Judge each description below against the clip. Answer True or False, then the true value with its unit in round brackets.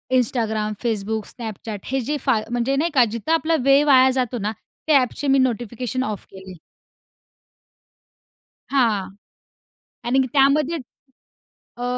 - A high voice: True (250 Hz)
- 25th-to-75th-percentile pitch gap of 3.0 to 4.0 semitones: True (3.7 semitones)